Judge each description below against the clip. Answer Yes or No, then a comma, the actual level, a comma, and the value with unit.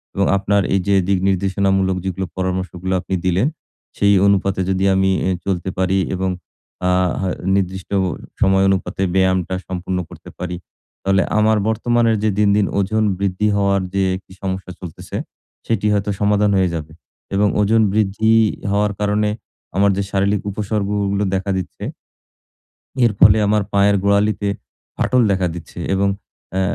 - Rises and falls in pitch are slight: Yes, narrow, 1.5 semitones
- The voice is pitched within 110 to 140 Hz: No, low, 100 Hz